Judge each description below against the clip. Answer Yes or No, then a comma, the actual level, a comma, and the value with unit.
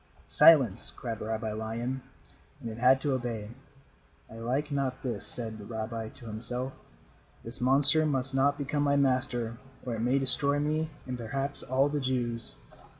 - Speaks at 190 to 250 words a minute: No, average, 160 wpm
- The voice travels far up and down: No, average, 3.2 semitones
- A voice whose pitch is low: Yes, low, 125 Hz